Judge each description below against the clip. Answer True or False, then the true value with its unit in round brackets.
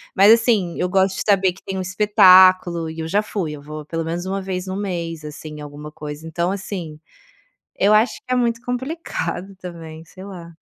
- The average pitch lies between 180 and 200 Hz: True (185 Hz)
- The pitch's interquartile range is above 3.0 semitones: True (3.5 semitones)